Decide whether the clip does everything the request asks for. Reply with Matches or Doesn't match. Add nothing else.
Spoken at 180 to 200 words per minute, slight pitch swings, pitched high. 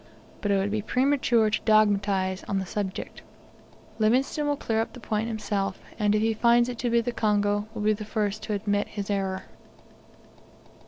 Matches